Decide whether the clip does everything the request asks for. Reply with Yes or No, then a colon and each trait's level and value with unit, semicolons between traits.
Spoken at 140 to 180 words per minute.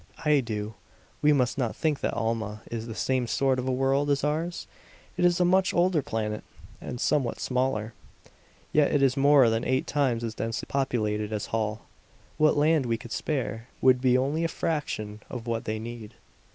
No: average, 190 wpm